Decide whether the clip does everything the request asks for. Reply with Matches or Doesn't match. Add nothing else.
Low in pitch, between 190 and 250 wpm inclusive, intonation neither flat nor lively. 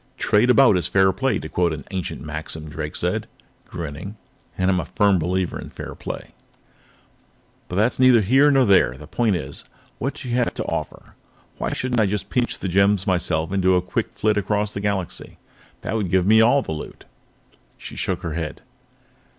Matches